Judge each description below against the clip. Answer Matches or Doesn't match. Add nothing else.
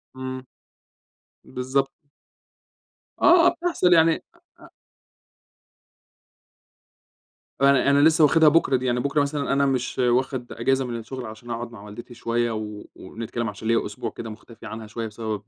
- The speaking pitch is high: Doesn't match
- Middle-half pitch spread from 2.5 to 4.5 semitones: Matches